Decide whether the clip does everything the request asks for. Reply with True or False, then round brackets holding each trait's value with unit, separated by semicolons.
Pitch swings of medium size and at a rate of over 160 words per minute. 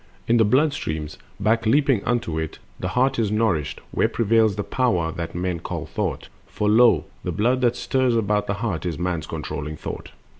False (5.7 semitones; 190 wpm)